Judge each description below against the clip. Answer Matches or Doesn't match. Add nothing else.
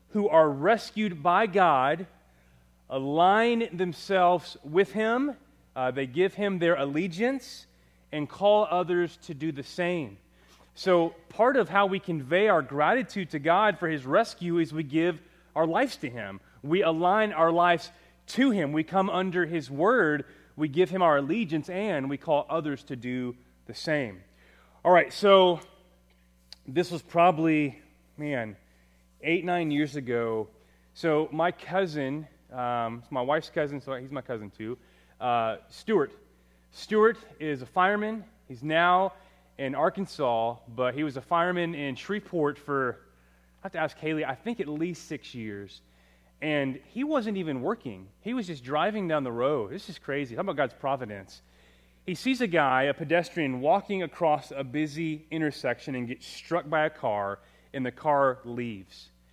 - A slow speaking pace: Doesn't match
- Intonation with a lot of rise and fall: Matches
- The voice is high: Doesn't match